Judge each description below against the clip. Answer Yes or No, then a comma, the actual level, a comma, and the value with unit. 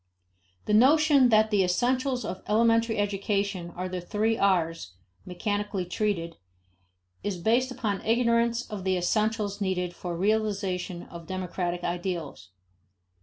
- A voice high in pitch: Yes, high, 200 Hz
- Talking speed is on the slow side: Yes, slow, 120 wpm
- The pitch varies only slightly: No, average, 3.8 semitones